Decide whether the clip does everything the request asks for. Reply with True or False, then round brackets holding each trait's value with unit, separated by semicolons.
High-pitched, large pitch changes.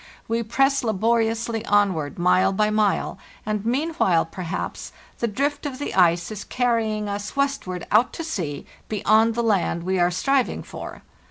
False (215 Hz; 4.1 semitones)